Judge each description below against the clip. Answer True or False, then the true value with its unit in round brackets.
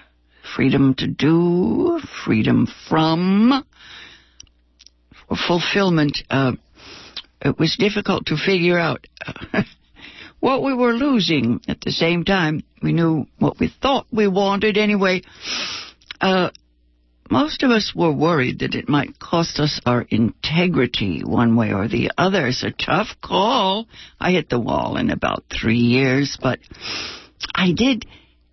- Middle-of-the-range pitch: True (160 Hz)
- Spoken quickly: False (135 wpm)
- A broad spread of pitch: True (8.0 semitones)